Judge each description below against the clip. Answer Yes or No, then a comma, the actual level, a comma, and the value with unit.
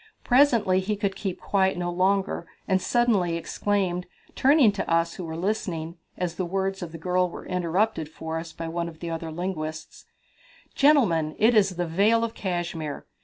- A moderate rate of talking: Yes, average, 175 wpm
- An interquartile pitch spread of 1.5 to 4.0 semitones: Yes, average, 3.3 semitones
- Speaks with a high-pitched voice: No, medium, 180 Hz